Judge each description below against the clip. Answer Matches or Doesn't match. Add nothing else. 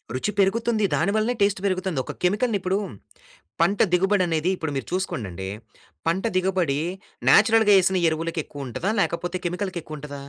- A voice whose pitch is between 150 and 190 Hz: Matches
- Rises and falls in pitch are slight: Doesn't match